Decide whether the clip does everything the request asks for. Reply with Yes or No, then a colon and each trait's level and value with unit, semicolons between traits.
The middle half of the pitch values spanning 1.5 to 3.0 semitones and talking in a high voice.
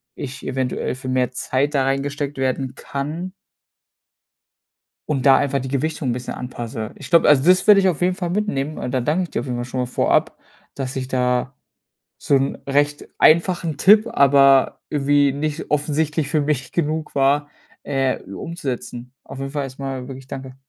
No: narrow, 2.6 semitones; medium, 140 Hz